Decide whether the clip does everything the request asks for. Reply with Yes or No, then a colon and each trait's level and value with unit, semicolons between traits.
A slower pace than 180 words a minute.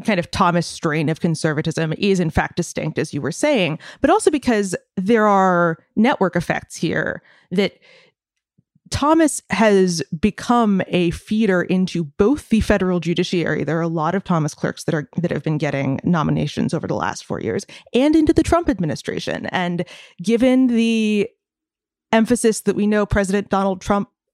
Yes: average, 165 wpm